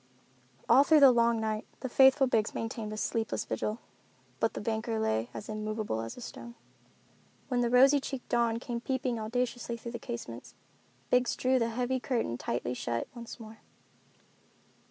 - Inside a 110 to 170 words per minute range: Yes, average, 165 wpm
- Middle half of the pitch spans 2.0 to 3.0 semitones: Yes, narrow, 2.5 semitones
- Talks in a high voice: Yes, high, 235 Hz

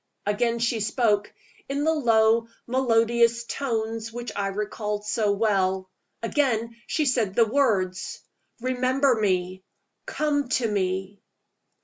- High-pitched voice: Yes, high, 225 Hz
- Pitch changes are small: No, average, 3.2 semitones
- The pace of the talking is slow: Yes, slow, 115 wpm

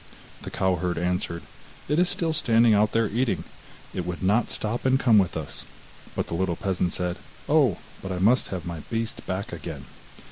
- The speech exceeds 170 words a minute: Yes, average, 190 wpm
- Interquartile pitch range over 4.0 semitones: Yes, average, 4.5 semitones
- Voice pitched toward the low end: Yes, very low, 95 Hz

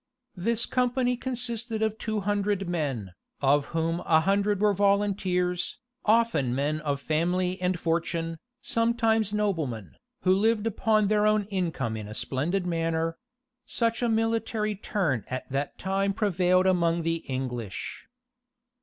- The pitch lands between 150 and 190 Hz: Yes, medium, 185 Hz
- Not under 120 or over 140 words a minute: Yes, slow, 135 wpm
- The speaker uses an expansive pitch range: No, average, 4.7 semitones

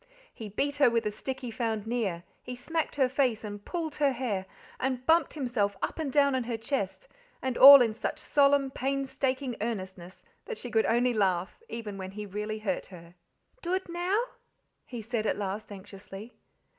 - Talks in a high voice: Yes, high, 235 Hz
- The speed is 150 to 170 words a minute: No, average, 180 wpm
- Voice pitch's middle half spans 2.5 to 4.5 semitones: No, average, 4.9 semitones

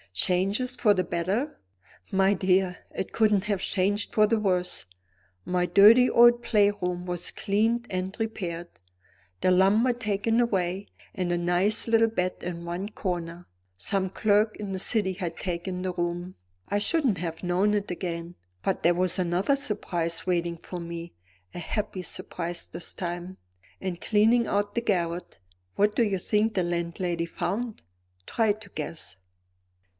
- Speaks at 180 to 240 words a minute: No, average, 155 wpm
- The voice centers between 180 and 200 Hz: Yes, high, 190 Hz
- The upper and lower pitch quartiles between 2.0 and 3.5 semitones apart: Yes, average, 3.1 semitones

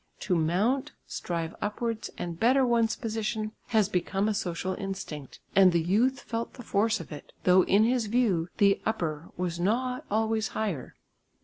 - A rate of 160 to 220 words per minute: Yes, average, 165 wpm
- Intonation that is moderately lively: Yes, average, 4.3 semitones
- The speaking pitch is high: Yes, high, 205 Hz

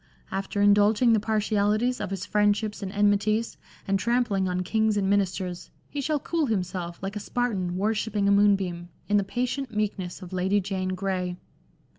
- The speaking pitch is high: Yes, high, 205 Hz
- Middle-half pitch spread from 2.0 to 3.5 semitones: Yes, narrow, 2.4 semitones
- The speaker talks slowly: No, average, 170 wpm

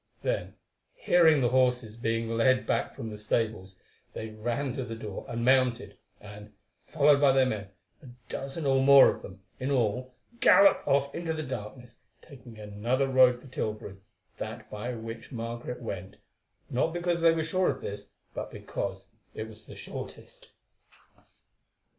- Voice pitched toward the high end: No, low, 125 Hz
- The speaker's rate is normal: Yes, average, 160 wpm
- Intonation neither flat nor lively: Yes, average, 3.8 semitones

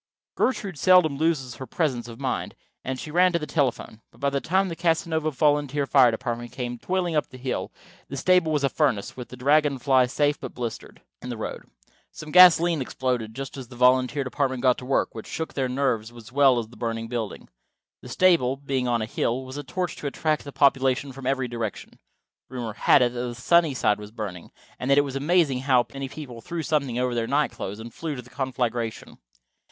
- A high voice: No, low, 130 Hz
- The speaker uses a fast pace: Yes, fast, 210 wpm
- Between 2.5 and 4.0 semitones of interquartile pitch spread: Yes, average, 3.6 semitones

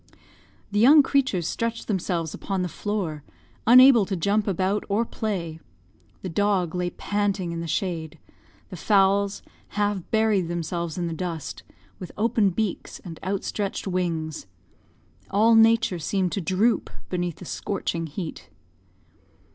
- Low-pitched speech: No, high, 190 Hz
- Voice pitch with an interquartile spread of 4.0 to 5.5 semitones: No, average, 3.5 semitones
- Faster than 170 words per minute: No, slow, 135 wpm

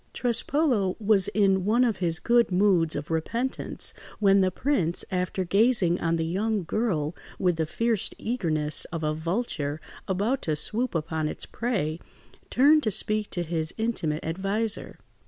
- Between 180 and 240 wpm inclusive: No, average, 155 wpm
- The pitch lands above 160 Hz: Yes, high, 190 Hz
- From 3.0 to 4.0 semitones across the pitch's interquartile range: No, wide, 5.5 semitones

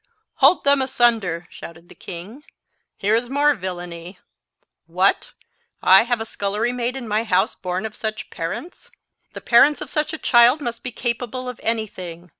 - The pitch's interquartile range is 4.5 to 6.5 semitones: Yes, average, 5.2 semitones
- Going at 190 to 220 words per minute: No, average, 170 wpm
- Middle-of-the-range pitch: No, high, 230 Hz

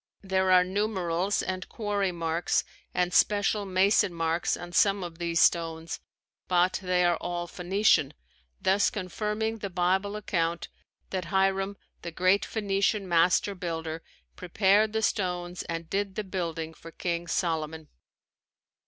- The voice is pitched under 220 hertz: Yes, medium, 185 Hz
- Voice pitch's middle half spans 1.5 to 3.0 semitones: Yes, average, 2.7 semitones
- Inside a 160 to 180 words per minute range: No, slow, 135 wpm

